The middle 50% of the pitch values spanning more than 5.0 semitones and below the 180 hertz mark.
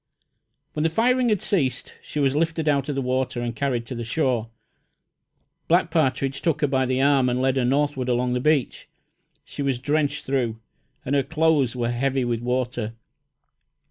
No: average, 3.2 semitones; low, 135 Hz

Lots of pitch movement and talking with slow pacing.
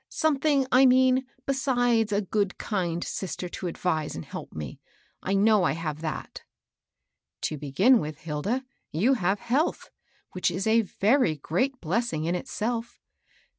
No: wide, 7.3 semitones; average, 155 wpm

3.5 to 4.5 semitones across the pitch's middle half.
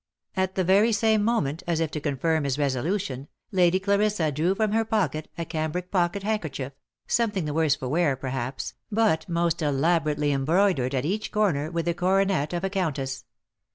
No: average, 5.1 semitones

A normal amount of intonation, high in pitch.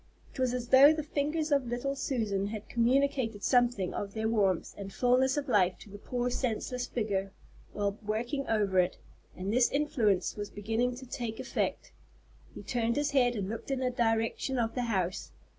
Yes: average, 4.0 semitones; high, 235 Hz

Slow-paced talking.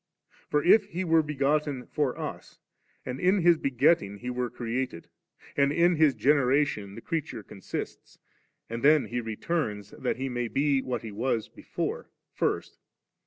No: average, 155 wpm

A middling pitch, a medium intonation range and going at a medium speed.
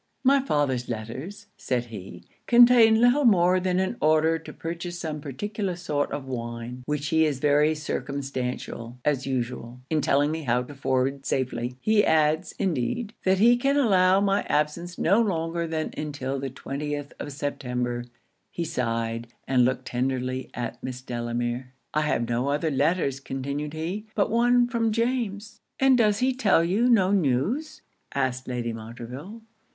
No: medium, 150 Hz; wide, 7.3 semitones; average, 155 wpm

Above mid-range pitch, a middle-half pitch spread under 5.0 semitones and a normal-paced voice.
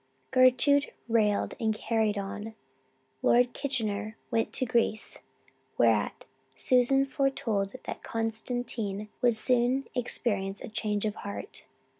No: high, 225 Hz; average, 3.0 semitones; slow, 110 wpm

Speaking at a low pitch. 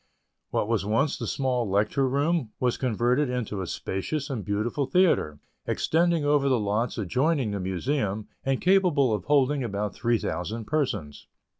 Yes: low, 125 Hz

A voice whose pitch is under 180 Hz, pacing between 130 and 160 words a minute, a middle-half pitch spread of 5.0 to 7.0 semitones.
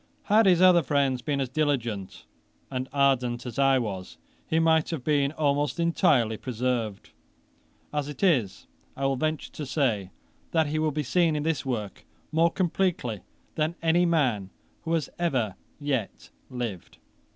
No: medium, 140 Hz; average, 155 wpm; average, 4.6 semitones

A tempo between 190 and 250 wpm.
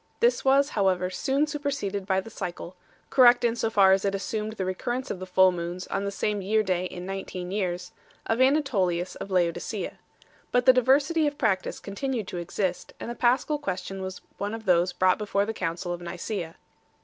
Yes: average, 195 wpm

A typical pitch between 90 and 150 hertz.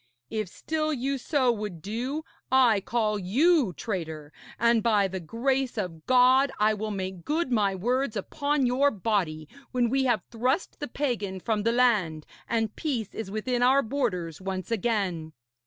No: high, 225 Hz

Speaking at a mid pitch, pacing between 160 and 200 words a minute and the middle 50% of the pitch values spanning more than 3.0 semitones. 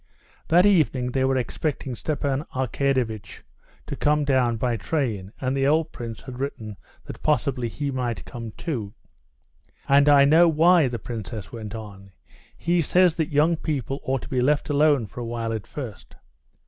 No: low, 130 Hz; average, 170 wpm; average, 4.3 semitones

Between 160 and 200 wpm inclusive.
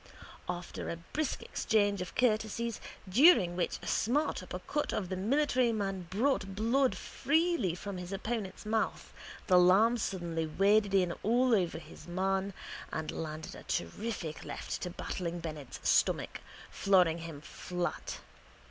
No: average, 140 wpm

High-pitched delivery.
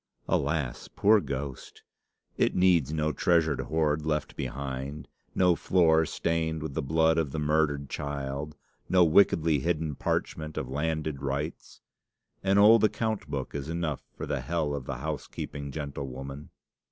No: very low, 75 Hz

